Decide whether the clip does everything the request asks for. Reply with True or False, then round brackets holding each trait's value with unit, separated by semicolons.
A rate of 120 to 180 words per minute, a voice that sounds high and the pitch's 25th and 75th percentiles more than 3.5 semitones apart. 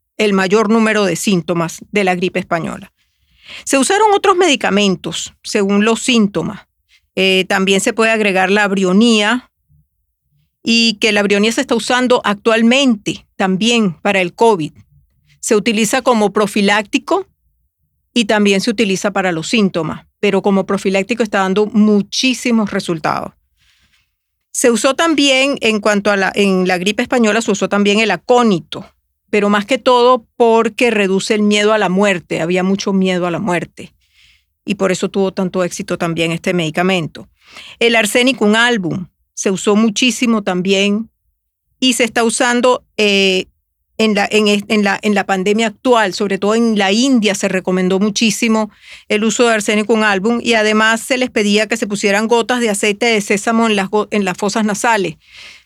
False (160 wpm; 210 Hz; 3.2 semitones)